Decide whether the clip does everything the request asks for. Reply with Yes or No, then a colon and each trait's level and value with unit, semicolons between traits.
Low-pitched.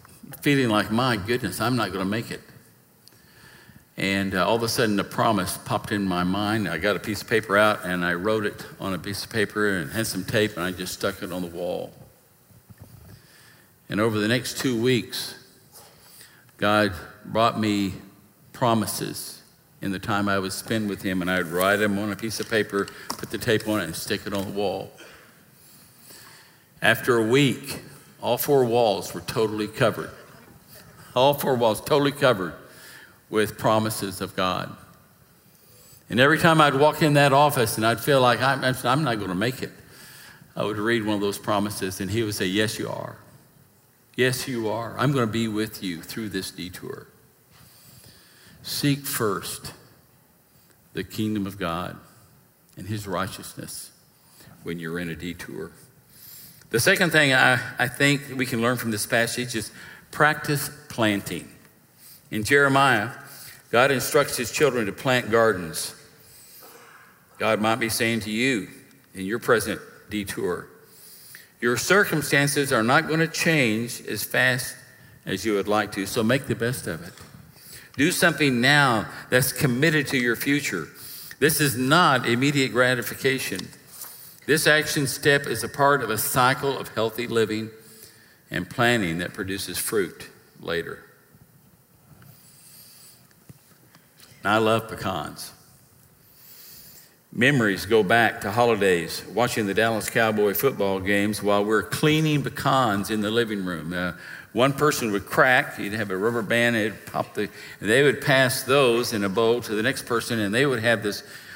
Yes: low, 115 Hz